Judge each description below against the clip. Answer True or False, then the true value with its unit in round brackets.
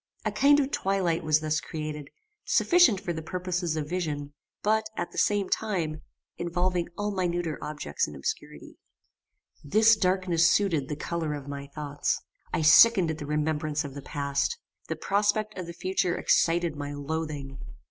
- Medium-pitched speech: True (165 Hz)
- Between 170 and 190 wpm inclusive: False (160 wpm)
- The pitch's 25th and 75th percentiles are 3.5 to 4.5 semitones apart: True (3.8 semitones)